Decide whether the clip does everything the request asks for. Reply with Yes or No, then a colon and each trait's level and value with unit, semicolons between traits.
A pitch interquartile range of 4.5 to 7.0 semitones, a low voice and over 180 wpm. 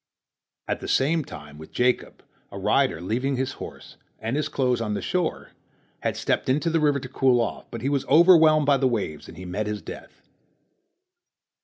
Yes: wide, 5.4 semitones; low, 130 Hz; average, 190 wpm